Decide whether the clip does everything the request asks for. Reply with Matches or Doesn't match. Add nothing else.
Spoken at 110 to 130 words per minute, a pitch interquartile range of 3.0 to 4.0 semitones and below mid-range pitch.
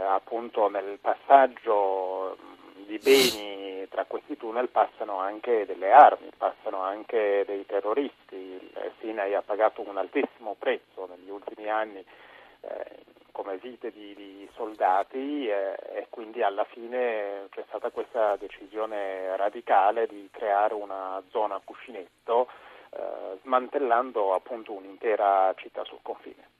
Matches